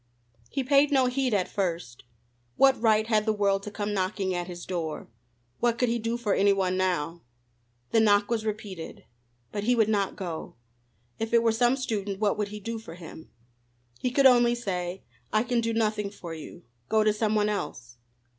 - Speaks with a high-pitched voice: Yes, high, 210 Hz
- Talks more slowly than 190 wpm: No, average, 195 wpm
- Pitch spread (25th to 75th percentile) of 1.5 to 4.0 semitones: Yes, average, 3.7 semitones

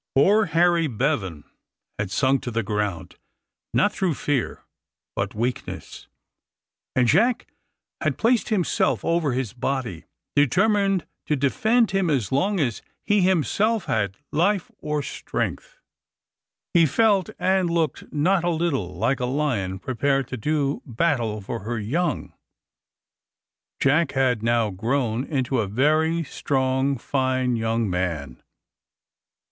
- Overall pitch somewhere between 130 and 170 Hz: Yes, low, 135 Hz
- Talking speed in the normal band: No, slow, 125 wpm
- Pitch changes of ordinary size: No, wide, 6.8 semitones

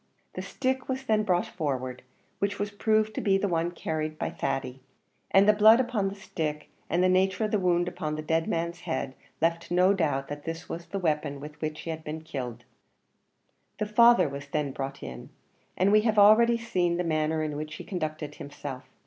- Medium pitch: Yes, medium, 170 Hz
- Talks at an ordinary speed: No, fast, 210 wpm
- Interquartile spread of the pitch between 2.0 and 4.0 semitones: No, average, 5.0 semitones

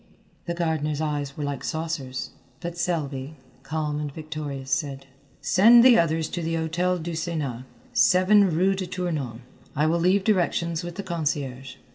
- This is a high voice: No, medium, 160 Hz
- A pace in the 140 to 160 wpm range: Yes, average, 155 wpm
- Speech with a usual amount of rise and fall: Yes, average, 3.3 semitones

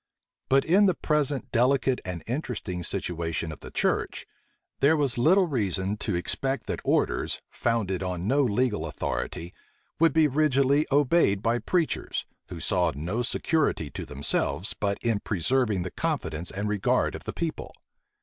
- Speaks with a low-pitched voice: Yes, low, 115 Hz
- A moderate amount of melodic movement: No, wide, 7.4 semitones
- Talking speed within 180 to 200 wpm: No, average, 150 wpm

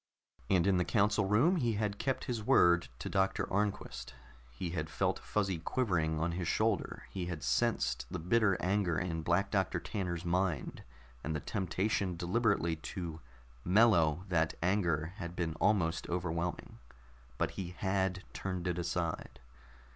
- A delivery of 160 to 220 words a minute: No, average, 150 wpm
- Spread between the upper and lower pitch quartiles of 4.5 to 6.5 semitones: No, average, 3.1 semitones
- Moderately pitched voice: No, very low, 90 Hz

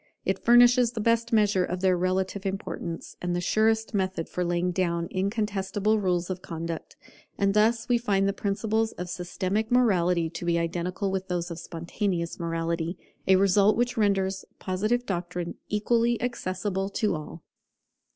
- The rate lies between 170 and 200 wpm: No, average, 155 wpm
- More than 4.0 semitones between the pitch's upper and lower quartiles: No, average, 3.4 semitones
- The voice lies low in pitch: No, high, 190 Hz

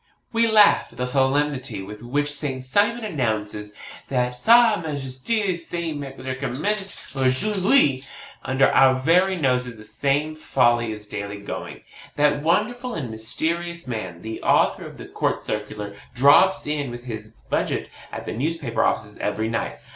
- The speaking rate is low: No, average, 145 wpm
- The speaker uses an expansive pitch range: Yes, wide, 6.2 semitones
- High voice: No, low, 135 Hz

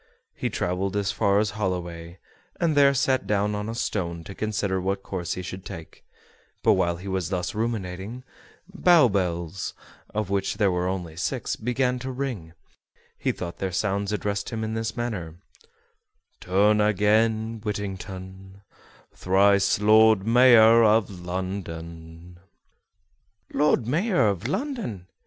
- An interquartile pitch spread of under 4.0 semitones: Yes, average, 3.4 semitones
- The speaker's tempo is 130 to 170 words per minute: Yes, average, 140 wpm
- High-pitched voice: No, low, 100 Hz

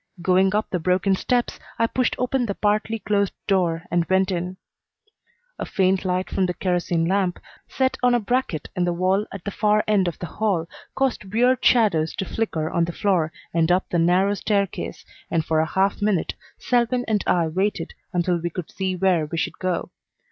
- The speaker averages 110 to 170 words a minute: No, average, 195 wpm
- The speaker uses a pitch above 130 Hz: Yes, high, 190 Hz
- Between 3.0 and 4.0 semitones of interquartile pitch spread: Yes, average, 3.3 semitones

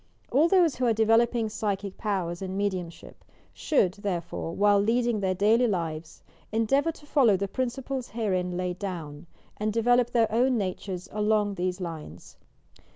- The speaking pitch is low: No, high, 205 Hz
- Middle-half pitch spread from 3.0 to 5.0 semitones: Yes, average, 4.4 semitones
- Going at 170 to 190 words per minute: No, average, 155 wpm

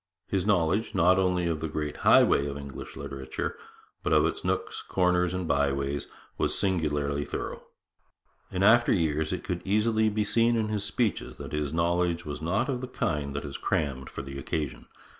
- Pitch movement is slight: No, wide, 5.4 semitones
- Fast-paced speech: No, average, 180 wpm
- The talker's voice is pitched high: No, very low, 85 Hz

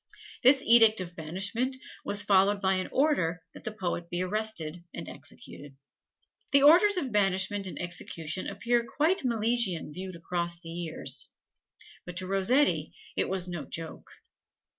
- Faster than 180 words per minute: No, average, 145 wpm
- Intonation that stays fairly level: No, average, 5.1 semitones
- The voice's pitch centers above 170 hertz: Yes, high, 190 Hz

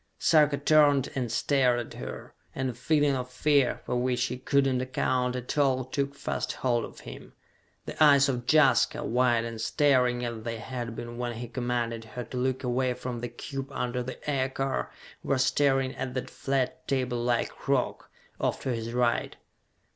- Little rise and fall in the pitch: Yes, narrow, 2.0 semitones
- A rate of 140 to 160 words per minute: No, average, 180 wpm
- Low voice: Yes, low, 125 Hz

